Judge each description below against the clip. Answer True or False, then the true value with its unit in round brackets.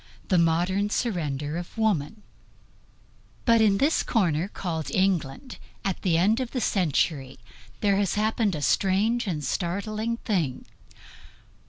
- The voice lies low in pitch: False (190 Hz)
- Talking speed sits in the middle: False (130 wpm)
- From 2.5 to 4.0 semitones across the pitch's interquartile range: False (4.9 semitones)